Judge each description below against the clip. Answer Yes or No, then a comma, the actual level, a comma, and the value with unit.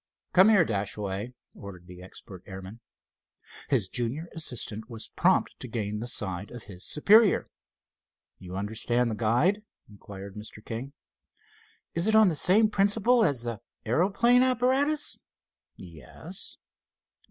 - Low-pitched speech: Yes, low, 120 Hz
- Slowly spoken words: Yes, slow, 130 wpm